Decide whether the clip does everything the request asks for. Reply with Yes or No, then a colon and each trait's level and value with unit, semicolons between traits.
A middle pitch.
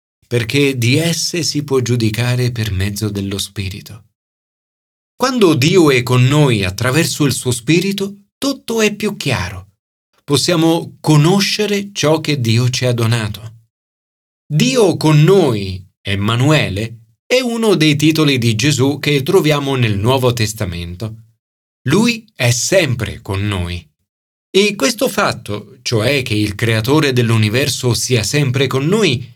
No: low, 125 Hz